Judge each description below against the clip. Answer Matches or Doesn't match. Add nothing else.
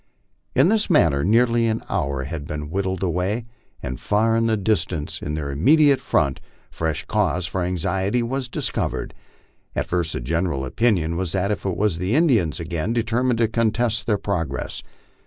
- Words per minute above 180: Doesn't match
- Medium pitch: Doesn't match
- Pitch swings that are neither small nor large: Doesn't match